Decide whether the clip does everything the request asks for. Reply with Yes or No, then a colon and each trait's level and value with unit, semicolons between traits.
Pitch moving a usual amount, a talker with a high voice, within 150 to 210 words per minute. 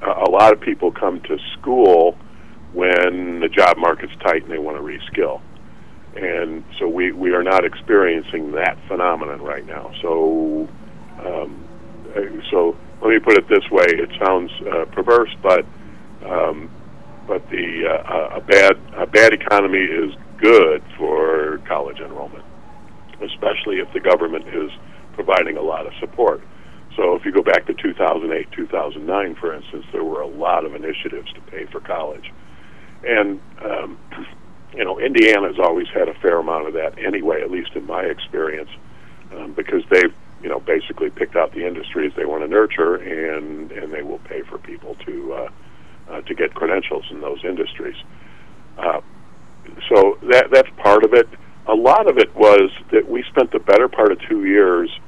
Yes: average, 4.4 semitones; very high, 395 Hz; average, 170 wpm